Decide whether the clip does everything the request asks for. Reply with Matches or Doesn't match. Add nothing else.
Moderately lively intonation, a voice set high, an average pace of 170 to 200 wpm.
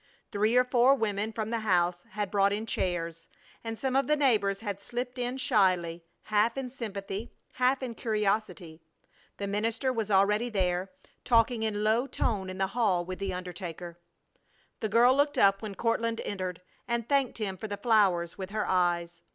Matches